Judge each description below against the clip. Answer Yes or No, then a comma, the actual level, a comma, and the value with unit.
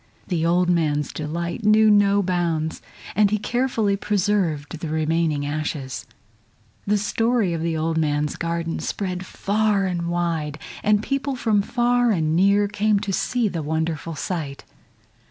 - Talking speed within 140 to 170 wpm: Yes, average, 145 wpm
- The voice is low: No, medium, 175 Hz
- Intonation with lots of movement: No, average, 4.6 semitones